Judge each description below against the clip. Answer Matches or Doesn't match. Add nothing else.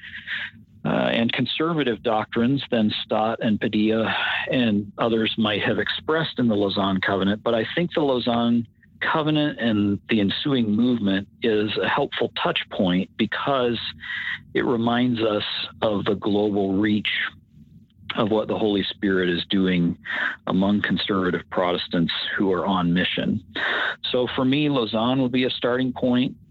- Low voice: Matches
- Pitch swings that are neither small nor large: Matches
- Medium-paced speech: Matches